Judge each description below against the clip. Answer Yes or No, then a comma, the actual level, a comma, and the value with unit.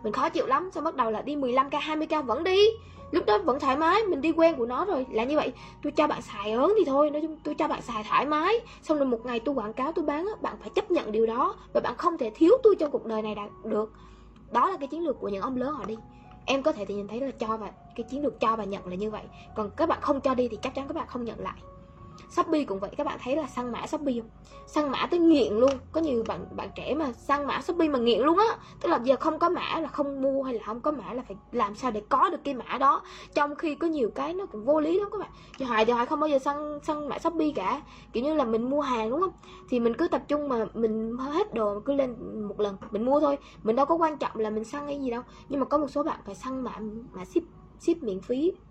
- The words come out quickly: Yes, fast, 295 wpm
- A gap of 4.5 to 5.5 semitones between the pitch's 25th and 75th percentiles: Yes, average, 5.1 semitones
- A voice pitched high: Yes, very high, 275 Hz